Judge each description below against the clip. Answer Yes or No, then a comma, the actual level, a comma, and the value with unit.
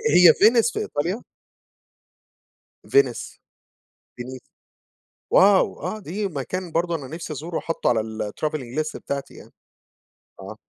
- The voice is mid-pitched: Yes, medium, 165 Hz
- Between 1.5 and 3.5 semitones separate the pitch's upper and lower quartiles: No, average, 5.1 semitones